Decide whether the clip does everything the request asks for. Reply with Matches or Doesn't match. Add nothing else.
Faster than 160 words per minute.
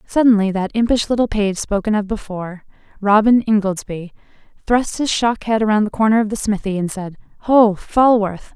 Matches